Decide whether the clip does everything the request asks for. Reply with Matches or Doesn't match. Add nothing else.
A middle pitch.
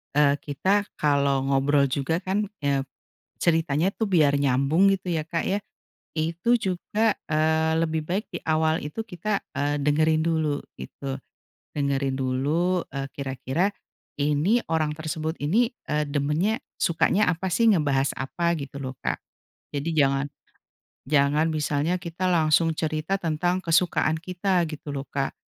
Matches